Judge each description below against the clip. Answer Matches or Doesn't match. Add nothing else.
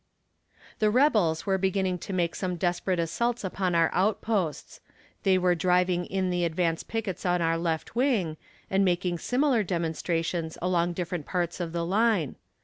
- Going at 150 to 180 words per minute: Matches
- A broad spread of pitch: Doesn't match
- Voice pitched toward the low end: Doesn't match